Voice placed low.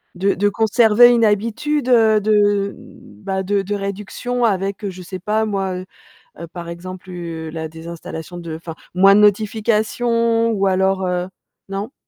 No: high, 200 Hz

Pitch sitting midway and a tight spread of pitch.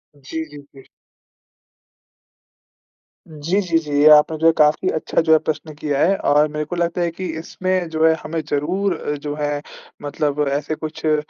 Yes: medium, 155 Hz; narrow, 2.0 semitones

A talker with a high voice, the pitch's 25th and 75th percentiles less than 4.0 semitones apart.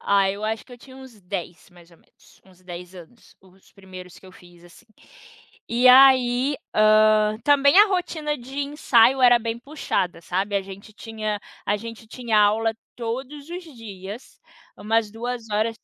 No: high, 225 Hz; average, 4.4 semitones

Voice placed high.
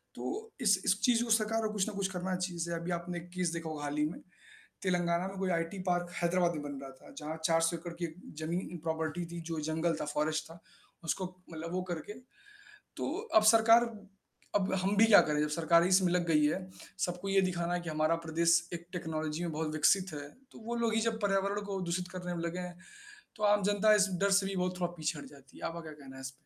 No: medium, 175 Hz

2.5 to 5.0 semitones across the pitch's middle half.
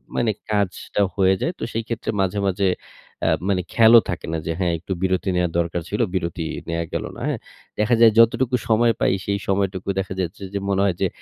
Yes: average, 3.5 semitones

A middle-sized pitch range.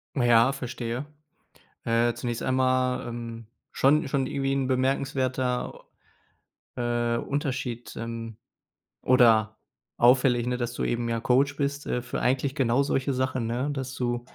No: narrow, 2.1 semitones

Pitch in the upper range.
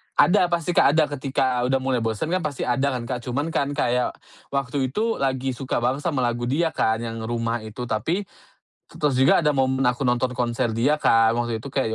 No: low, 130 Hz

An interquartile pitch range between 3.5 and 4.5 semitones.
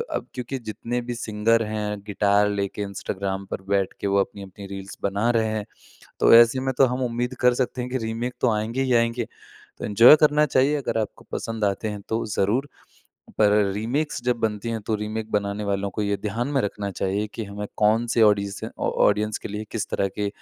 No: average, 2.8 semitones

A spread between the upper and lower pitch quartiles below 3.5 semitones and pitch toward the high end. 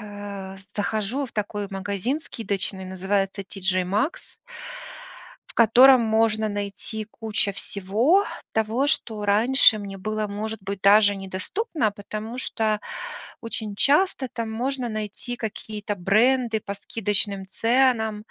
Yes: narrow, 2.5 semitones; high, 215 Hz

